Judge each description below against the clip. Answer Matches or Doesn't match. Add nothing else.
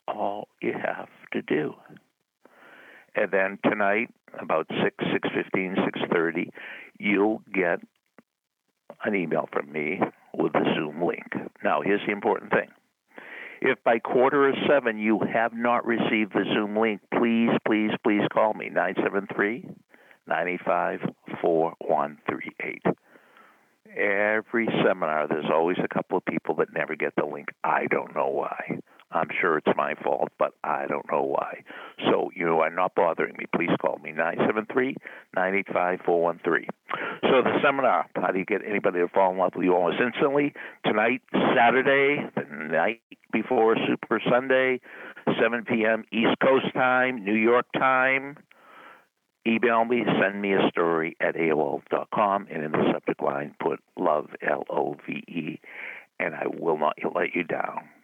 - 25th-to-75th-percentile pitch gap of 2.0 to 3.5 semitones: Doesn't match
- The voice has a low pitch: Matches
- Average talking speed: Matches